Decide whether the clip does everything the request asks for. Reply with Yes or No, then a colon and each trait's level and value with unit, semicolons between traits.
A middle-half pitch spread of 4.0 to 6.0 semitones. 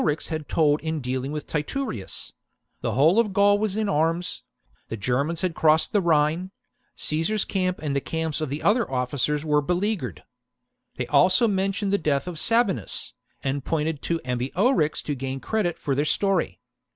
Yes: average, 5.1 semitones